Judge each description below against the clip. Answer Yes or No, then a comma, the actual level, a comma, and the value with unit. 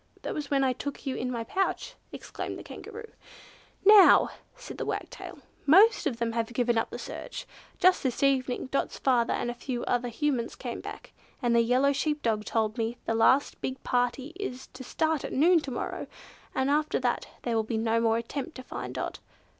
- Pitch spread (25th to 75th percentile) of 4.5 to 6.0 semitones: No, average, 3.8 semitones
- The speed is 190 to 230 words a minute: Yes, average, 200 wpm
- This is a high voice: Yes, very high, 255 Hz